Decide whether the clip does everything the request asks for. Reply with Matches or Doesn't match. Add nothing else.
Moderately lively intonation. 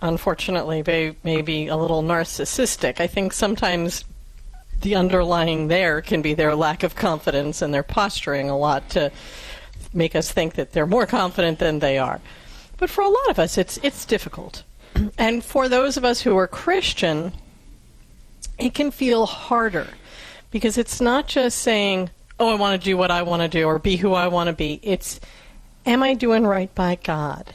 Doesn't match